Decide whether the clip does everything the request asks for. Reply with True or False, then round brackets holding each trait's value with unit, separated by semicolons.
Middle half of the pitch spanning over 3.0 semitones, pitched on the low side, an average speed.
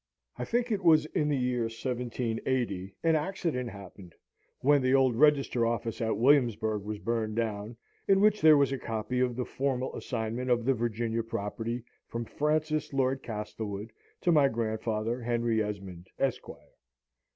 True (3.6 semitones; 120 Hz; 155 wpm)